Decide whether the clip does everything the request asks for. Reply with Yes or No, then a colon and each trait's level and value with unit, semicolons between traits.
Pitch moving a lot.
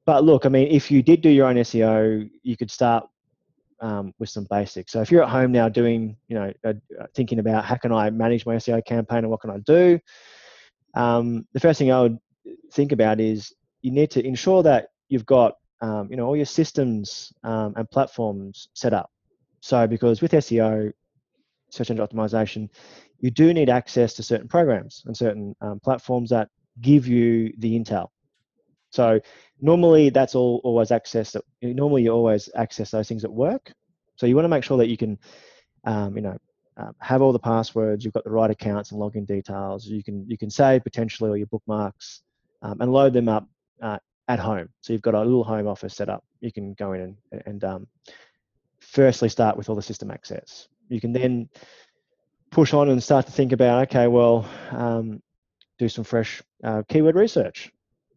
No: average, 3.1 semitones